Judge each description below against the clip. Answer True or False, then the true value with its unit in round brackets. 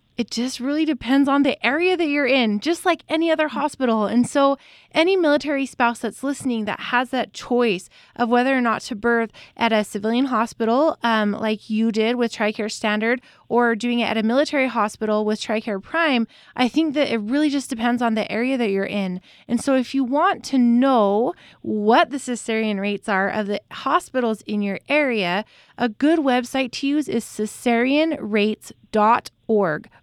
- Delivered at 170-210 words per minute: True (180 wpm)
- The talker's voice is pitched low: False (240 Hz)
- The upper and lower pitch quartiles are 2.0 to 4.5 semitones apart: True (4.1 semitones)